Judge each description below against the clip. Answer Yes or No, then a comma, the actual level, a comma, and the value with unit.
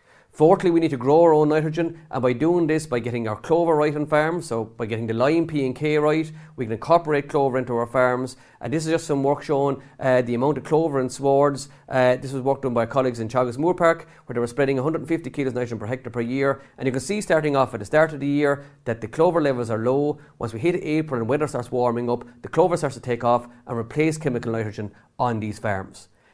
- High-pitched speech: No, low, 135 Hz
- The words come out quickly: Yes, fast, 255 wpm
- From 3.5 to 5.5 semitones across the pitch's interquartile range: Yes, average, 4.1 semitones